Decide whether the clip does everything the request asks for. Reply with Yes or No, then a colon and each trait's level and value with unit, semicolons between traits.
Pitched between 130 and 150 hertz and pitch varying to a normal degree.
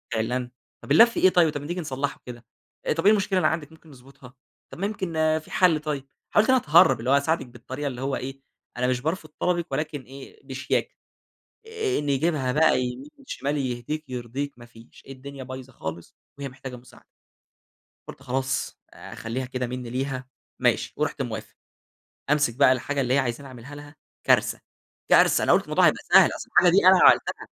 Yes: low, 135 Hz; average, 3.7 semitones